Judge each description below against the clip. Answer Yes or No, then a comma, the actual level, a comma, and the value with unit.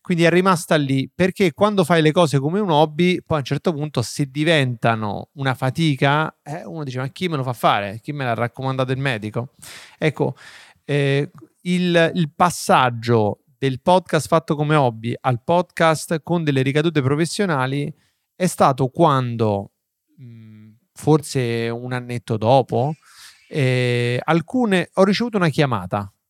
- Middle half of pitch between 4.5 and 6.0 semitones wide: Yes, average, 5.1 semitones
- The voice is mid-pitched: Yes, medium, 145 Hz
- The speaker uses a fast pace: No, average, 150 wpm